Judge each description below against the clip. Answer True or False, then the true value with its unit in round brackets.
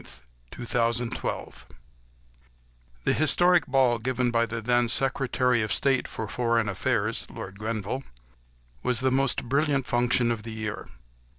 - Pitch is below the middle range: True (120 Hz)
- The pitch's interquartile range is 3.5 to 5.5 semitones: False (2.9 semitones)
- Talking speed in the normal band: False (125 wpm)